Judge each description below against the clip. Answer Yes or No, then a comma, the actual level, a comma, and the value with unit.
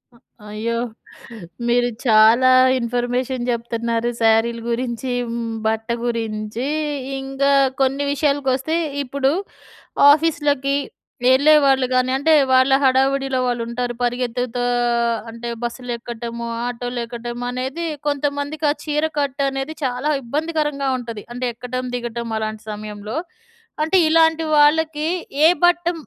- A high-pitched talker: Yes, very high, 255 Hz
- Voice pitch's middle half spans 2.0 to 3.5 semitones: Yes, average, 3.1 semitones